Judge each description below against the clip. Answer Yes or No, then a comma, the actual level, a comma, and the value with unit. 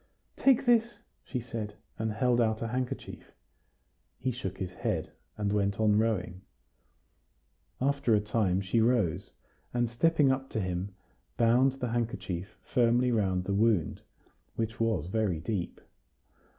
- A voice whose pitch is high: No, low, 110 Hz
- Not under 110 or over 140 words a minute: Yes, slow, 135 wpm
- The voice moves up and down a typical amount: Yes, average, 3.8 semitones